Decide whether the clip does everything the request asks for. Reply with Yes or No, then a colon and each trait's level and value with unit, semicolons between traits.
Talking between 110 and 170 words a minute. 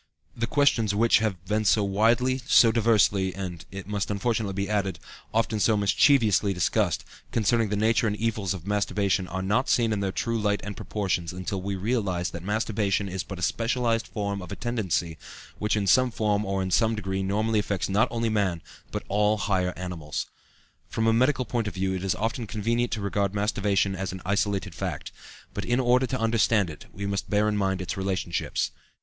No: average, 200 wpm